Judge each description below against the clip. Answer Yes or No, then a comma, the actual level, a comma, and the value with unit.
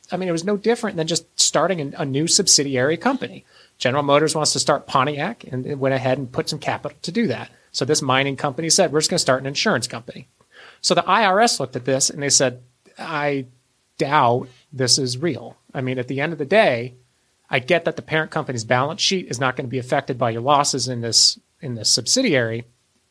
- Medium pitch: Yes, medium, 145 Hz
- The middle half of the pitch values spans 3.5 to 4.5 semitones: Yes, average, 3.9 semitones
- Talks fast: Yes, fast, 225 wpm